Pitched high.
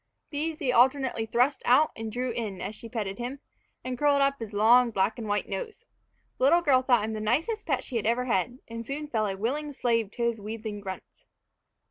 Yes: high, 240 Hz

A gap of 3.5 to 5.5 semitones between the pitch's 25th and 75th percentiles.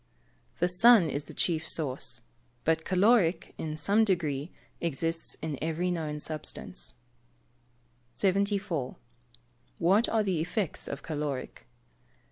Yes: average, 4.2 semitones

